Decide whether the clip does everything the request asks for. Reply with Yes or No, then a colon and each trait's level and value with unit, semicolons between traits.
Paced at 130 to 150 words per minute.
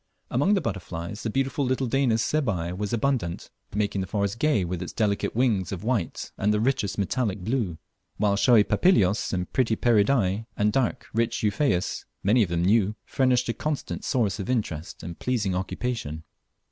No: average, 170 wpm